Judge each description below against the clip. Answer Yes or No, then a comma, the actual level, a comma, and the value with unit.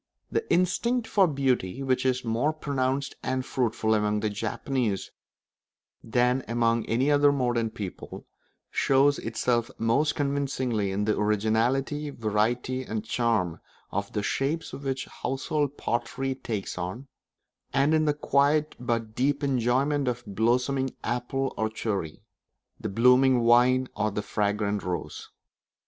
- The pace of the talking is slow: Yes, slow, 130 wpm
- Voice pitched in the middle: No, low, 125 Hz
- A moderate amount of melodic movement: Yes, average, 3.8 semitones